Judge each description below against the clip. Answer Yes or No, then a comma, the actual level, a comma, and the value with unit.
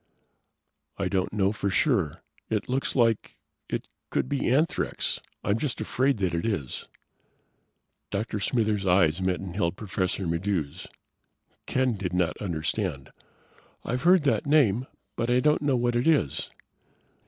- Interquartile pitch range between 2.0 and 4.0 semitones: No, wide, 5.5 semitones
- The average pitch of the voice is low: Yes, low, 105 Hz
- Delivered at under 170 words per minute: Yes, average, 140 wpm